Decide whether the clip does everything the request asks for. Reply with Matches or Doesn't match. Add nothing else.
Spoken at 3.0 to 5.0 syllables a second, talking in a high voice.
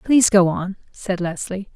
Matches